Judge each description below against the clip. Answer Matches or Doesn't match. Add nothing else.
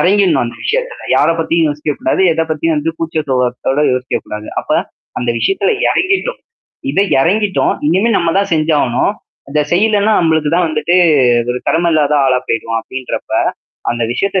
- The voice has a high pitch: Doesn't match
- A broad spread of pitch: Matches